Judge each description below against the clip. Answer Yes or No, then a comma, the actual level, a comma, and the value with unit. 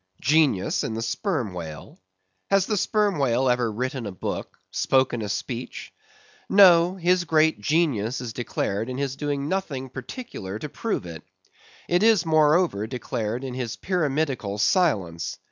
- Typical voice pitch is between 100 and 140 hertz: Yes, low, 135 Hz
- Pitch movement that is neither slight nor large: No, wide, 7.0 semitones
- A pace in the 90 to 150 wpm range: Yes, average, 145 wpm